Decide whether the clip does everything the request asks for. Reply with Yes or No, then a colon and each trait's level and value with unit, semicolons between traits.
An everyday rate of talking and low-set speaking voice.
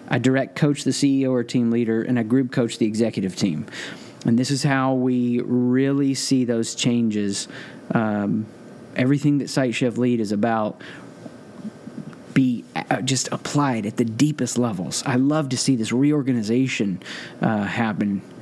Yes: average, 155 wpm; low, 125 Hz